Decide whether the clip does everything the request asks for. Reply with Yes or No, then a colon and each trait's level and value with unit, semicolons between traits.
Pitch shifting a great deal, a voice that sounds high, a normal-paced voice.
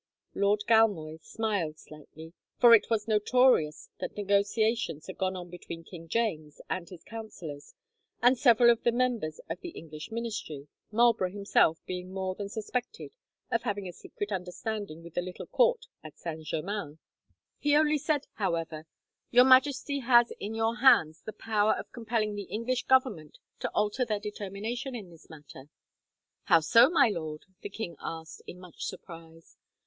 Yes: wide, 5.9 semitones; high, 205 Hz; average, 160 wpm